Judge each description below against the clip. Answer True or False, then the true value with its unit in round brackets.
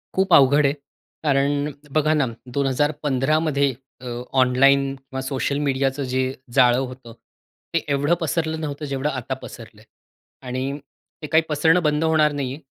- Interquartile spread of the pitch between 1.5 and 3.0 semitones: True (2.4 semitones)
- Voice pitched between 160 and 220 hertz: False (140 Hz)